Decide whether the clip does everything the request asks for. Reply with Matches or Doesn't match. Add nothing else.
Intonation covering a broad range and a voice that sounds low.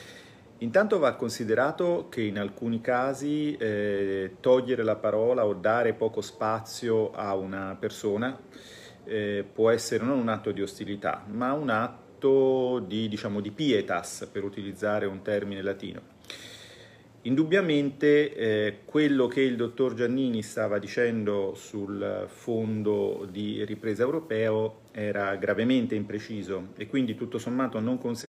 Doesn't match